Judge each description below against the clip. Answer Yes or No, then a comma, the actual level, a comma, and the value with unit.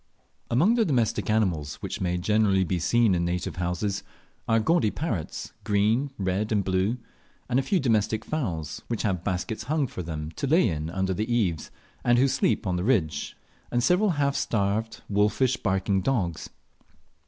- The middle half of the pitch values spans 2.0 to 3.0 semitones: No, average, 5.0 semitones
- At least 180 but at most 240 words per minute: No, average, 165 wpm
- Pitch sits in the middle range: No, low, 105 Hz